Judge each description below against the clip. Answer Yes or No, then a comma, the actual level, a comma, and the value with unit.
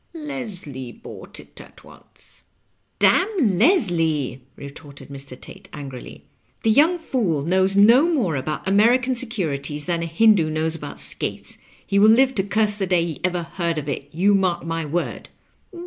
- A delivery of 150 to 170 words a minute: Yes, average, 165 wpm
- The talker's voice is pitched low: No, medium, 180 Hz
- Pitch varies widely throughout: Yes, wide, 6.4 semitones